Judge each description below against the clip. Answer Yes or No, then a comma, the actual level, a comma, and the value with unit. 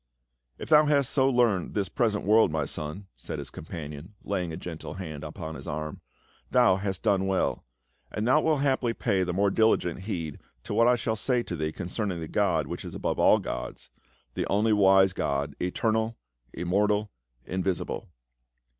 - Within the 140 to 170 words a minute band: No, average, 195 wpm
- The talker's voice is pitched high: No, very low, 95 Hz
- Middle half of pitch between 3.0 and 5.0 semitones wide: No, wide, 5.5 semitones